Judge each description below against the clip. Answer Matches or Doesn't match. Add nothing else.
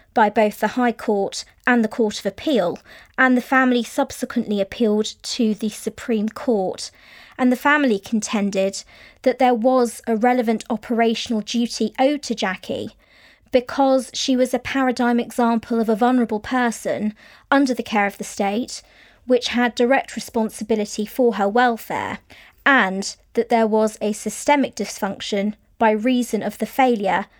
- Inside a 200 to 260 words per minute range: Doesn't match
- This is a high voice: Matches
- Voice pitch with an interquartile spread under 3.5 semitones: Matches